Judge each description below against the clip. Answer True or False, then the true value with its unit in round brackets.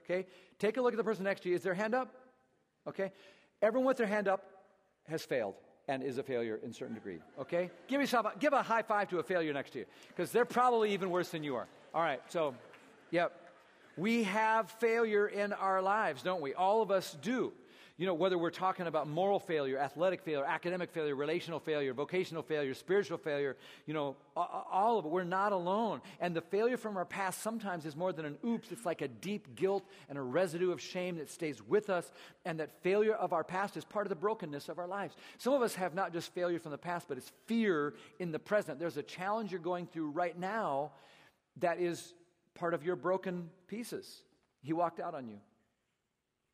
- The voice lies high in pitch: False (180 Hz)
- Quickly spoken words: True (220 wpm)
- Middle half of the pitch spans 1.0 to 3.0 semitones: False (3.9 semitones)